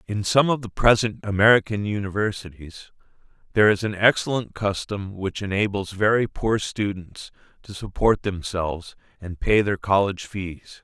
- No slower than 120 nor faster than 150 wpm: Yes, average, 140 wpm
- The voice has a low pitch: Yes, low, 100 Hz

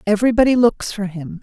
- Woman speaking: Yes, female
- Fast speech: No, average, 170 wpm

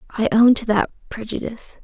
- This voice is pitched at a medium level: No, high, 225 Hz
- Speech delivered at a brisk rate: No, average, 165 wpm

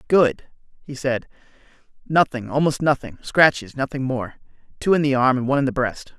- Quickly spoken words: No, average, 165 wpm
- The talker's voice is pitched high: No, low, 135 Hz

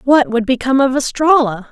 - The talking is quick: No, average, 175 wpm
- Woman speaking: Yes, female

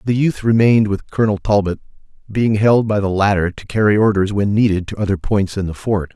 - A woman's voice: No, male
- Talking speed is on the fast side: Yes, fast, 215 wpm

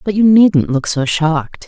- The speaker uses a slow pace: No, fast, 215 wpm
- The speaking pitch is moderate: Yes, medium, 170 Hz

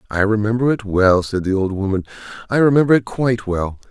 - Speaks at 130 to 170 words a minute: No, average, 200 wpm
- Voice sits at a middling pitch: No, low, 110 Hz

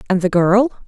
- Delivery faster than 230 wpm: No, fast, 205 wpm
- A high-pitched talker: Yes, high, 200 Hz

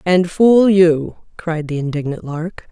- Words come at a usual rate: Yes, average, 155 wpm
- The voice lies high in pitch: No, medium, 170 Hz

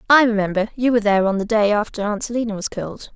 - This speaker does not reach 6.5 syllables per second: No, 7.3 syllables/s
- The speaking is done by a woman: Yes, female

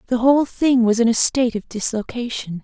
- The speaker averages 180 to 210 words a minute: Yes, fast, 205 wpm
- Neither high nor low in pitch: No, high, 235 Hz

